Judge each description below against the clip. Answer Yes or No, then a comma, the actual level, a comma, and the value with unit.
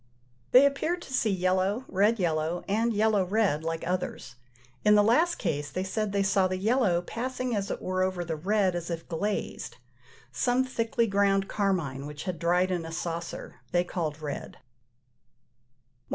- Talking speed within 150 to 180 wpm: Yes, average, 170 wpm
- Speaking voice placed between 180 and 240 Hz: Yes, high, 190 Hz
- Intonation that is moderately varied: Yes, average, 4.0 semitones